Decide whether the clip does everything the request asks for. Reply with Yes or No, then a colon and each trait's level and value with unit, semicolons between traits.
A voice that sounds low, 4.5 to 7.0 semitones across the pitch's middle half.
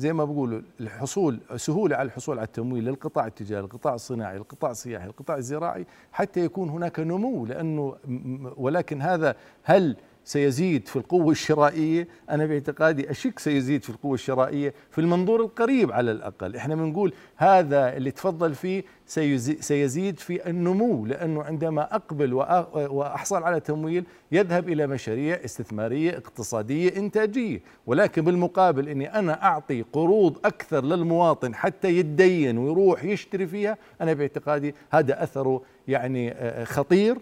No: medium, 150 Hz; average, 4.9 semitones